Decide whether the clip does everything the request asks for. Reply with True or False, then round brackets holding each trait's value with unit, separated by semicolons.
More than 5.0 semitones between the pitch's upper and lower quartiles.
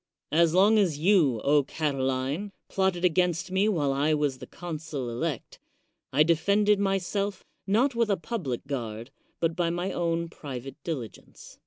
True (5.4 semitones)